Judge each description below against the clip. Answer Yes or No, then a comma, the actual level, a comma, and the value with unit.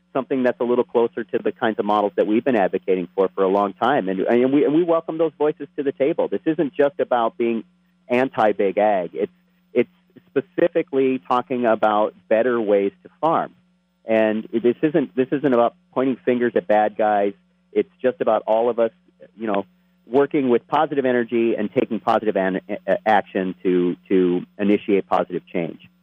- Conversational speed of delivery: Yes, average, 180 wpm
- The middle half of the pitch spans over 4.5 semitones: Yes, wide, 5.6 semitones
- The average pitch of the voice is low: Yes, low, 120 Hz